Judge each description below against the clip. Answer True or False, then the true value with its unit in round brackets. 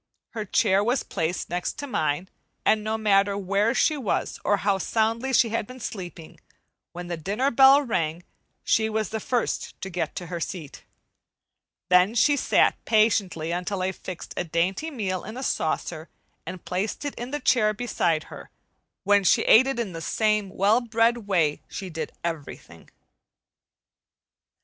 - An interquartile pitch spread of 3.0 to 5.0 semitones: True (4.4 semitones)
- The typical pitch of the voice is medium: False (205 Hz)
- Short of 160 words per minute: False (165 wpm)